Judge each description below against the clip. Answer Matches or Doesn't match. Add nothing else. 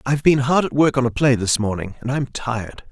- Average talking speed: Doesn't match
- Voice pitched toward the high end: Doesn't match